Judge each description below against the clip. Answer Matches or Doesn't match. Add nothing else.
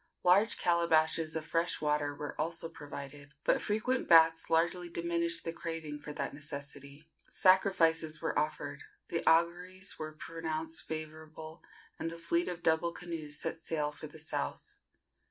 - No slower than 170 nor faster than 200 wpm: Doesn't match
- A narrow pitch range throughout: Matches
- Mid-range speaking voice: Matches